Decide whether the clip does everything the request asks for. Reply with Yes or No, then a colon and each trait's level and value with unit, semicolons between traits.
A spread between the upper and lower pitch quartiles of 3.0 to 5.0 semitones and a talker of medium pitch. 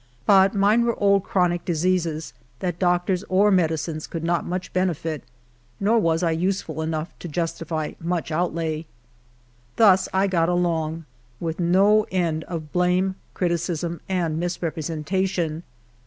No: narrow, 2.5 semitones; medium, 175 Hz